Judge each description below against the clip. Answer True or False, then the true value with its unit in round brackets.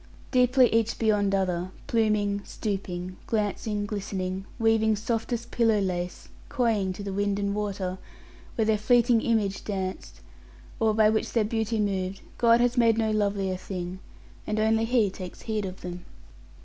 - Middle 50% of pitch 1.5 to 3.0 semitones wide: True (2.6 semitones)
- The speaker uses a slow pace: False (150 wpm)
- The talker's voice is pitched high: True (210 Hz)